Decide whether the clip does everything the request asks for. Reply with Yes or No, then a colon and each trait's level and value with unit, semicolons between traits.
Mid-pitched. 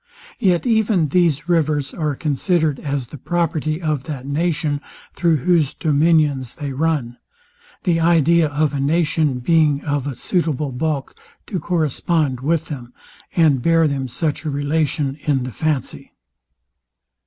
Yes: medium, 150 Hz